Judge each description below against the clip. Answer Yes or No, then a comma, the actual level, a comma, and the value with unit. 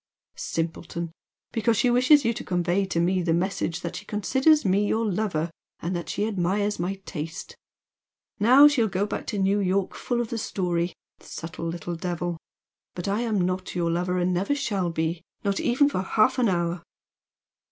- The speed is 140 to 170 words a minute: No, average, 180 wpm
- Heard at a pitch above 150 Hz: Yes, high, 190 Hz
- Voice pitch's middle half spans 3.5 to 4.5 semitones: Yes, average, 4.0 semitones